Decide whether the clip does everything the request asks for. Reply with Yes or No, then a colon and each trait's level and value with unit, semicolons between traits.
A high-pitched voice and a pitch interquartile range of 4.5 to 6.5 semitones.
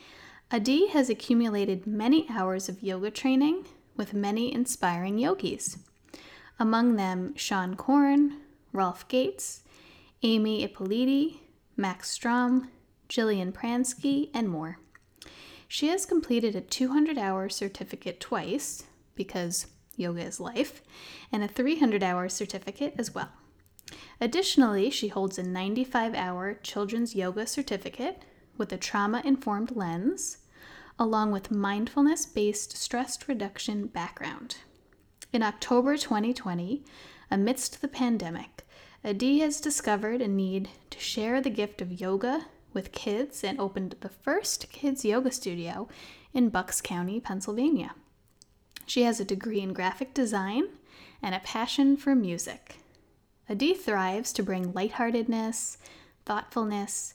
Yes: high, 225 Hz; average, 5.2 semitones